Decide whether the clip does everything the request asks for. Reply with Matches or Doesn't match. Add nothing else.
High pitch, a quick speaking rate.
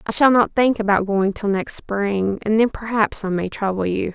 Matches